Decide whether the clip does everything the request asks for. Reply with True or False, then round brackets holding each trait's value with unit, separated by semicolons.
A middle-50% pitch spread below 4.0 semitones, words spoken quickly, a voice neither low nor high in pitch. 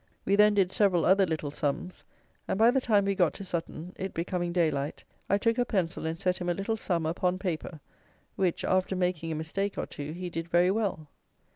True (3.1 semitones; 215 wpm; 180 Hz)